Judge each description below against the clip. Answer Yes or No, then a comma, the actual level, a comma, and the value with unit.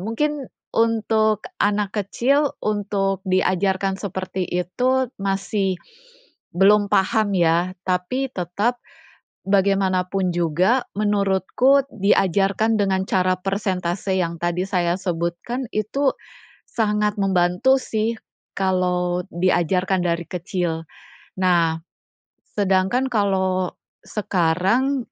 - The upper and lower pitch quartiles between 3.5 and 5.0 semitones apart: No, average, 2.9 semitones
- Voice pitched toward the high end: Yes, high, 195 Hz